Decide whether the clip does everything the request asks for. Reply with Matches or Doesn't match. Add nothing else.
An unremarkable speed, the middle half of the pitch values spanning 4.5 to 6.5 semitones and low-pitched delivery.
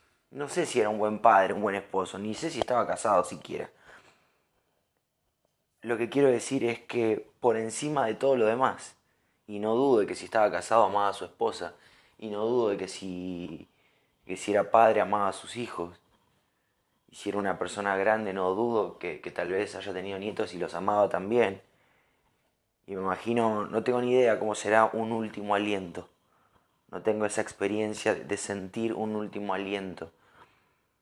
Doesn't match